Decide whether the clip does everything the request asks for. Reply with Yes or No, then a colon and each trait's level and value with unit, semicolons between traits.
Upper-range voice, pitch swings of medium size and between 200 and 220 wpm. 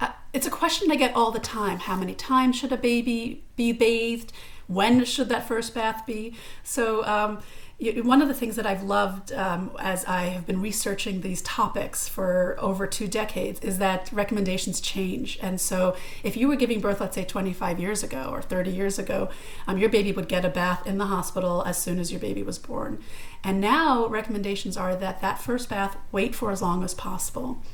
Yes: high, 205 Hz; average, 3.5 semitones; fast, 205 wpm